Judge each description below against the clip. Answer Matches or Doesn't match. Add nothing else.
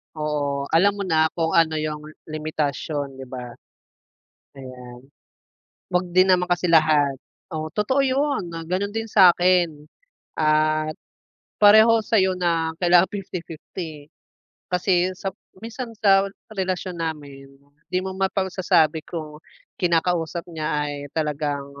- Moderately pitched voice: Matches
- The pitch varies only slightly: Doesn't match